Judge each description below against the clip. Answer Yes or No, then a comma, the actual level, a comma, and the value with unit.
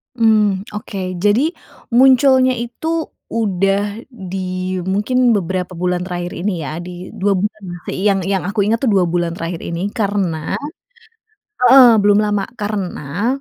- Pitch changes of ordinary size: Yes, average, 3.6 semitones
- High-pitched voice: Yes, high, 200 Hz